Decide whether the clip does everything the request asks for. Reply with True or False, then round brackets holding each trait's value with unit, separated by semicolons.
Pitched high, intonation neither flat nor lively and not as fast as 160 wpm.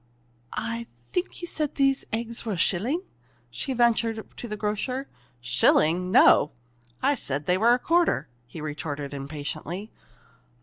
False (220 Hz; 8.3 semitones; 140 wpm)